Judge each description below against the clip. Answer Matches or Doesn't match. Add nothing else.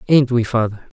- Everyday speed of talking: Matches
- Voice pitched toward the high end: Doesn't match